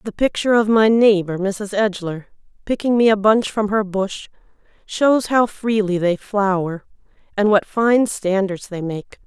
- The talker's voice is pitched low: No, high, 205 Hz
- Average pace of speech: Yes, average, 160 wpm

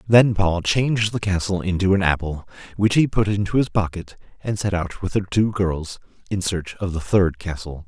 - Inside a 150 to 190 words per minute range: No, fast, 205 wpm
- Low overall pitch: Yes, very low, 95 Hz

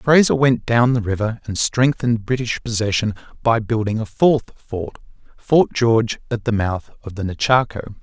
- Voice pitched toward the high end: No, low, 115 Hz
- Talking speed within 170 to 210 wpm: No, average, 155 wpm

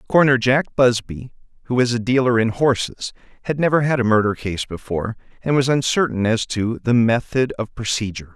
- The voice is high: No, low, 120 Hz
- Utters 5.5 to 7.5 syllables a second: Yes, 5.7 syllables/s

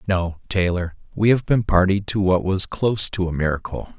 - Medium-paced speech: Yes, average, 195 wpm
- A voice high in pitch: No, very low, 95 Hz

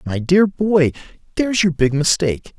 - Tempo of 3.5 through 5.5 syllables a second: Yes, 5.1 syllables/s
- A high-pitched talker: No, medium, 165 Hz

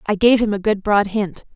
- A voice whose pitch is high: Yes, high, 205 Hz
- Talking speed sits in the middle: No, fast, 270 wpm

